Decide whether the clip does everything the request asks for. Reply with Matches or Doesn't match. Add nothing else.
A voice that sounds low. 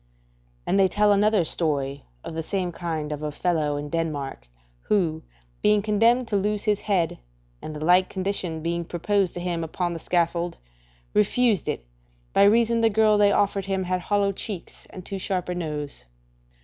Doesn't match